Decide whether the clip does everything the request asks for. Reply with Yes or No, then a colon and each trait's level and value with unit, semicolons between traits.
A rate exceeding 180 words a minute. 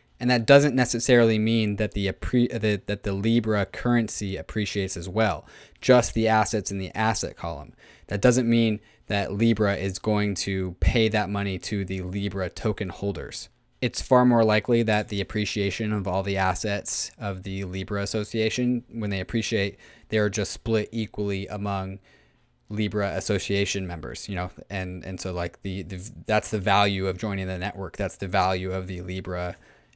No: average, 170 wpm